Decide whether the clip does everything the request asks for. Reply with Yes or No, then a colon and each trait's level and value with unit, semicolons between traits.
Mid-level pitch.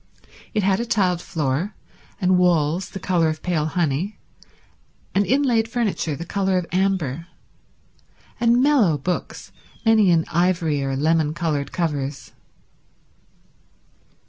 Yes: medium, 175 Hz